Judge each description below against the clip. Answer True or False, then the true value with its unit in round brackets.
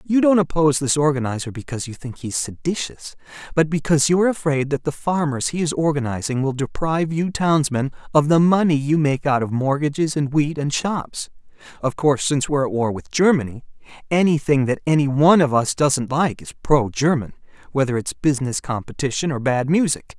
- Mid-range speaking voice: True (145 Hz)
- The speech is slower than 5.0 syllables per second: False (5.6 syllables/s)